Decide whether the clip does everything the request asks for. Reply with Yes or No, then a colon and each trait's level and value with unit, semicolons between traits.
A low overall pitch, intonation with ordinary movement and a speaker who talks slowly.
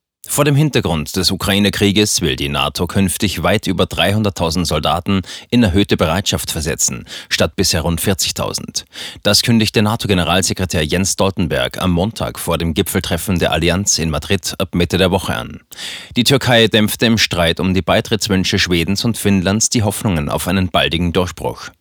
No: very low, 95 Hz; average, 3.5 semitones; average, 155 wpm